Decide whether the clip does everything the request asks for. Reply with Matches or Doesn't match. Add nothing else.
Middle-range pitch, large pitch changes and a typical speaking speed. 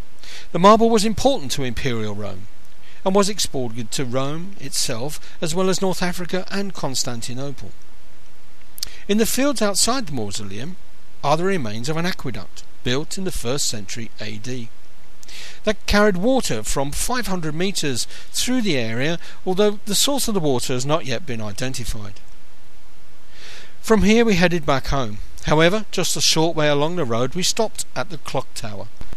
Matches